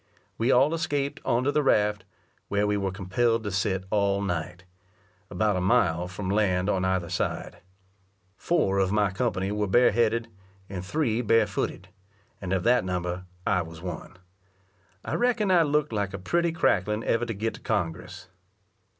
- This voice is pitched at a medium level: No, low, 100 Hz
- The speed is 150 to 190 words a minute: Yes, average, 165 wpm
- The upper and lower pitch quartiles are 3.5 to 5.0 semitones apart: Yes, average, 4.2 semitones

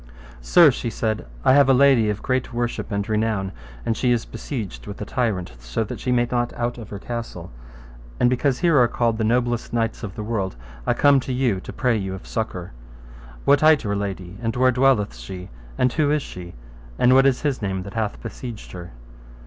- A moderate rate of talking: No, fast, 215 wpm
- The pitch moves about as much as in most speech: Yes, average, 4.0 semitones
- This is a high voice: No, low, 115 Hz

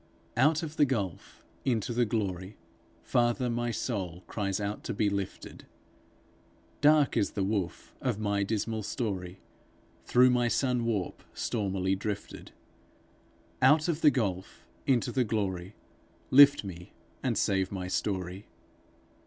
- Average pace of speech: No, slow, 130 wpm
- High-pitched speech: No, low, 105 Hz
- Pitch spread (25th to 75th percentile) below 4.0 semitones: No, average, 4.4 semitones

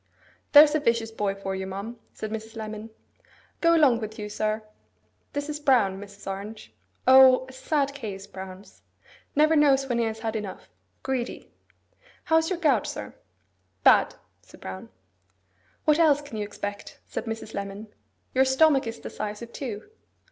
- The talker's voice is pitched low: No, high, 225 Hz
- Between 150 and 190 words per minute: Yes, average, 165 wpm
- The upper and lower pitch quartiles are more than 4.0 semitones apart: Yes, average, 5.0 semitones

